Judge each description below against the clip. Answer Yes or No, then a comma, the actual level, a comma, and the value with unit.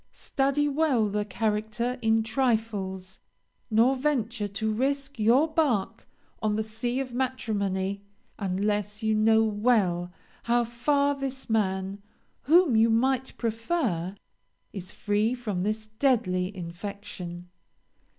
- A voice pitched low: No, high, 220 Hz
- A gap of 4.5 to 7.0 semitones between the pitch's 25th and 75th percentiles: No, average, 3.8 semitones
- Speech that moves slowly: Yes, slow, 115 wpm